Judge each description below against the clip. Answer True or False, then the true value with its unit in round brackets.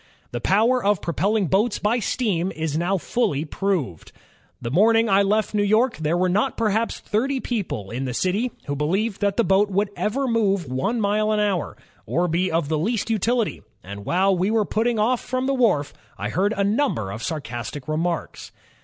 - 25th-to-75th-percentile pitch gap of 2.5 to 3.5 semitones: False (5.3 semitones)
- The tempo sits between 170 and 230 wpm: True (190 wpm)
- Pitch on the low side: False (200 Hz)